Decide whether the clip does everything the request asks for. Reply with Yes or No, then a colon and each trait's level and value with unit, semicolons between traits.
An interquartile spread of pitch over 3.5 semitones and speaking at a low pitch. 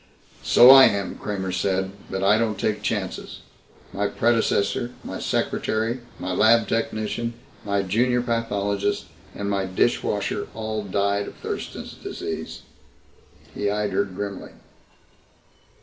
No: narrow, 2.4 semitones; low, 105 Hz